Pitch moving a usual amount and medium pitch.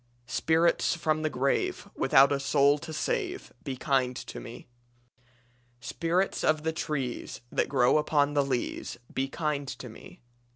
Yes: average, 3.0 semitones; medium, 145 Hz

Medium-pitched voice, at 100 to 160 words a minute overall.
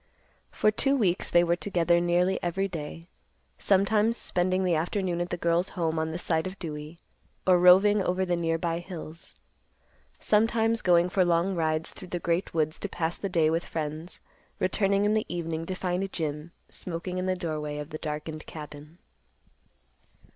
No: medium, 175 Hz; average, 170 wpm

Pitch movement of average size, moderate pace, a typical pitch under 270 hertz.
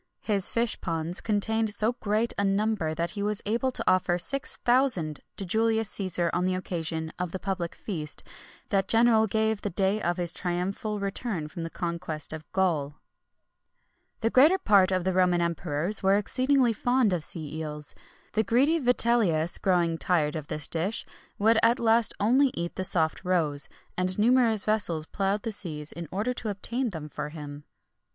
Yes: average, 4.9 semitones; average, 175 wpm; high, 190 Hz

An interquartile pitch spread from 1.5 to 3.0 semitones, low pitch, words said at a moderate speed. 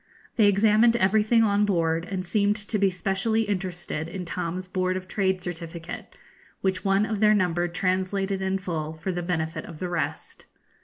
No: narrow, 2.5 semitones; high, 190 Hz; average, 170 wpm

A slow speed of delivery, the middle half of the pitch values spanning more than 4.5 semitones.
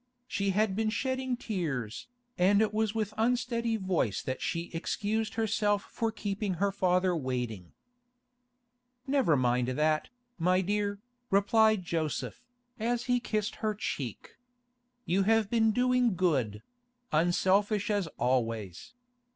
Yes: slow, 120 wpm; average, 5.3 semitones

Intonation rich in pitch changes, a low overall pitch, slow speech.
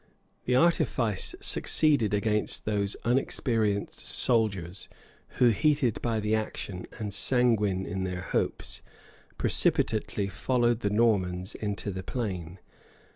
No: average, 3.5 semitones; low, 105 Hz; slow, 110 wpm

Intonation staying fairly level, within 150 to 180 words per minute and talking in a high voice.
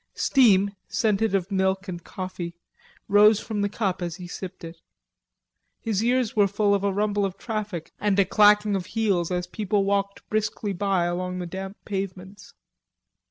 Yes: narrow, 2.2 semitones; average, 170 wpm; high, 200 Hz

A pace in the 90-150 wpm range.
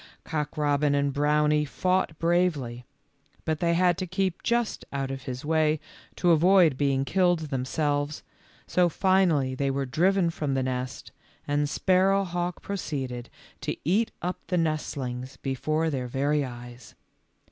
Yes: average, 145 wpm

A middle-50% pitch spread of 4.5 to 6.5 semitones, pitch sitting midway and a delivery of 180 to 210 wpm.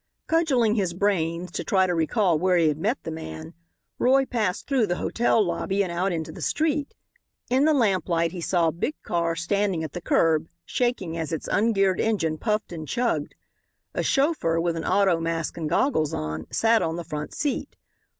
Yes: average, 5.3 semitones; medium, 180 Hz; average, 190 wpm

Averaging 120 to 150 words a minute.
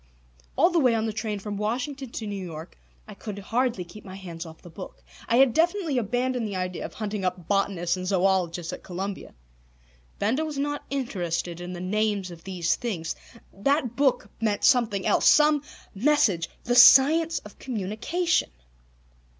No: average, 170 wpm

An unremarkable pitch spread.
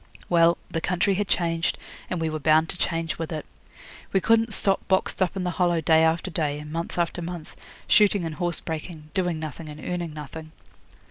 No: narrow, 2.2 semitones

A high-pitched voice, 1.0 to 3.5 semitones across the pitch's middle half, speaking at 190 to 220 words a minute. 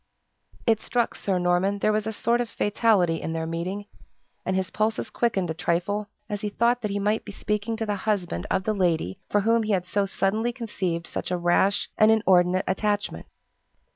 Yes: high, 200 Hz; average, 3.2 semitones; average, 200 wpm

